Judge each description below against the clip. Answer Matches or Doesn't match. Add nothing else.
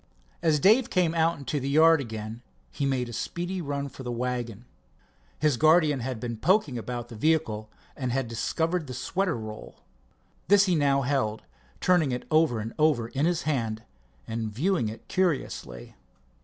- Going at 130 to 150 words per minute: Doesn't match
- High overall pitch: Doesn't match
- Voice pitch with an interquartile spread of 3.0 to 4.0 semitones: Doesn't match